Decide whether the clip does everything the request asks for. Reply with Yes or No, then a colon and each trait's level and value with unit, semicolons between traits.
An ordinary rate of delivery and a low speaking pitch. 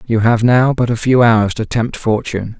No: fast, 230 wpm; low, 115 Hz